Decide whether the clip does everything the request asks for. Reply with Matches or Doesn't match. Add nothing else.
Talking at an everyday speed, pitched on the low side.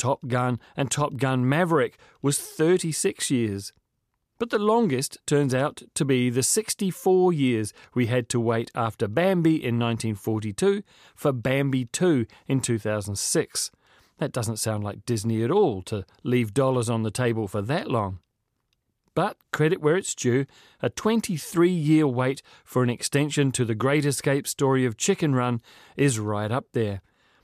Matches